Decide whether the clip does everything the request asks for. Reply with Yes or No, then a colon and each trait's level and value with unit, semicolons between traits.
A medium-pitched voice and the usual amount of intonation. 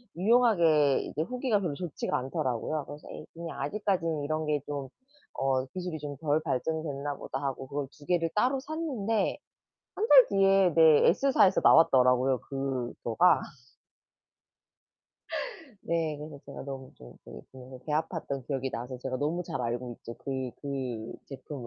Yes: medium, 150 Hz; average, 4.7 semitones